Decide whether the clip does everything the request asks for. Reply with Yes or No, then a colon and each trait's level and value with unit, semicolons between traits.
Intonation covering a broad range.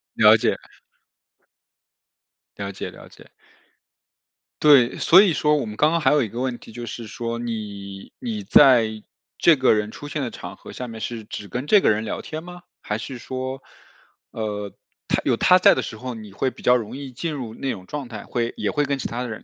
No: average, 5.0 semitones